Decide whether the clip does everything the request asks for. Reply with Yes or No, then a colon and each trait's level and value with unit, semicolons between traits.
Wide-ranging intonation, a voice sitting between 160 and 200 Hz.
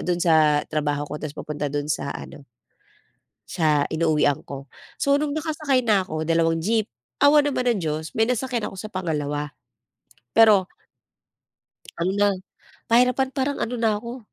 Yes: wide, 8.1 semitones; medium, 185 Hz